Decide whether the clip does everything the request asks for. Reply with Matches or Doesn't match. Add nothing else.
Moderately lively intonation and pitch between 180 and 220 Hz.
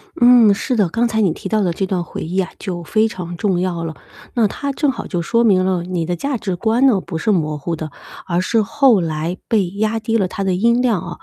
Matches